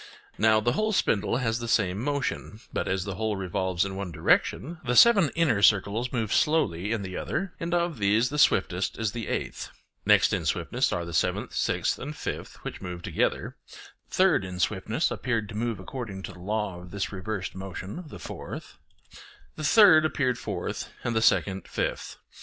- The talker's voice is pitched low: Yes, low, 110 Hz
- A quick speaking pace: No, average, 185 wpm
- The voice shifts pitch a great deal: Yes, wide, 6.0 semitones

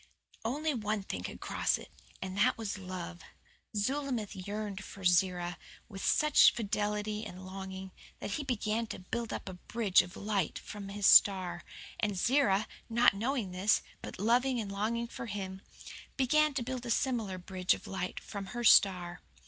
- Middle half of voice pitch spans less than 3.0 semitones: No, average, 3.7 semitones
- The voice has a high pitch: Yes, high, 205 Hz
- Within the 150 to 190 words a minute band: Yes, average, 165 wpm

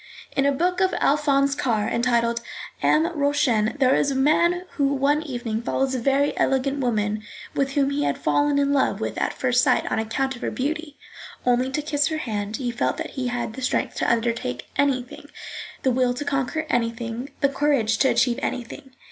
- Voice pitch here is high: Yes, very high, 265 Hz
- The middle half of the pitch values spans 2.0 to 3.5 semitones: Yes, average, 2.9 semitones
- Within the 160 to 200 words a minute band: Yes, average, 195 wpm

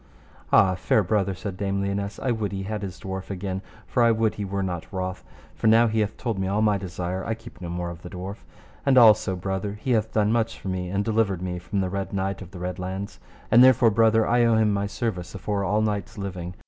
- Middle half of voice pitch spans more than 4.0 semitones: No, average, 2.8 semitones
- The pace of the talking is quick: Yes, fast, 245 wpm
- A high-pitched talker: No, low, 100 Hz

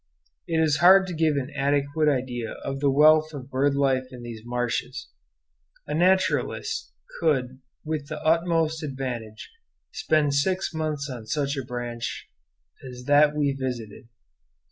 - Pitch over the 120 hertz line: Yes, medium, 140 Hz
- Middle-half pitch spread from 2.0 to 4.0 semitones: Yes, average, 3.4 semitones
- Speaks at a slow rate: No, average, 145 wpm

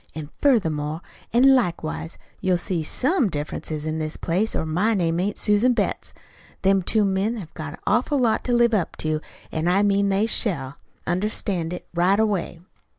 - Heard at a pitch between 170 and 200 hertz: Yes, high, 190 Hz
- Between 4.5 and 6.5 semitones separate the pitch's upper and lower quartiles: Yes, average, 5.2 semitones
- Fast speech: No, average, 175 wpm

